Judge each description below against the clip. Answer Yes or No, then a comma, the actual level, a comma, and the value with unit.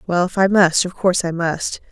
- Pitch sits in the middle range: Yes, medium, 180 Hz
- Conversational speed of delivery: No, fast, 250 wpm